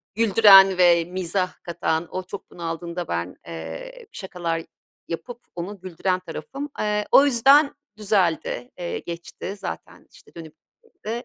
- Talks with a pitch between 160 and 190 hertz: Yes, medium, 185 Hz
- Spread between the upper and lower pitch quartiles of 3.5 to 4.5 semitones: Yes, average, 3.8 semitones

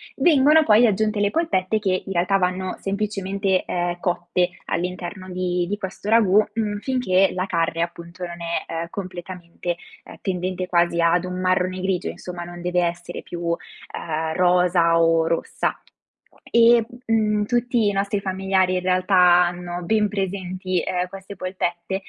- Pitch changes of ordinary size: No, narrow, 2.3 semitones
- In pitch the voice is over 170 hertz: Yes, medium, 185 Hz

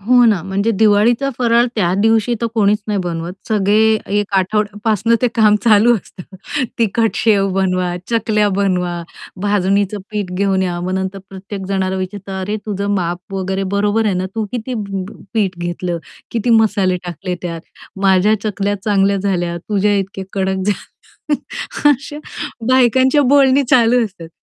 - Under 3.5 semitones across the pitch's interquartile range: Yes, average, 2.9 semitones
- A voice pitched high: Yes, high, 200 Hz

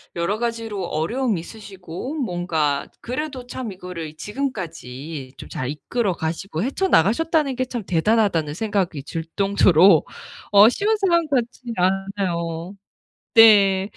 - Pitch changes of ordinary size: No, wide, 6.1 semitones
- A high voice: Yes, high, 195 Hz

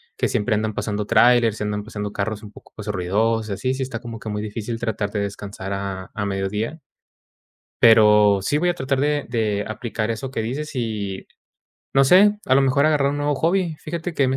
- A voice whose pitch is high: No, low, 115 Hz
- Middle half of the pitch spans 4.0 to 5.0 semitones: Yes, average, 4.6 semitones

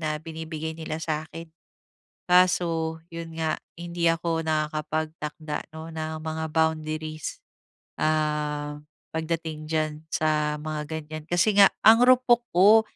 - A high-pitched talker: No, medium, 160 Hz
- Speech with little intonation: Yes, narrow, 1.3 semitones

